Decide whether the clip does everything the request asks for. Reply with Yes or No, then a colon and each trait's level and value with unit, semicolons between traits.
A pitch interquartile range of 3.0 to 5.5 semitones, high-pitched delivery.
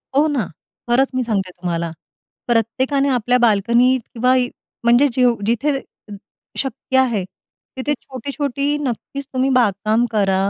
Yes: average, 3.5 semitones; high, 245 Hz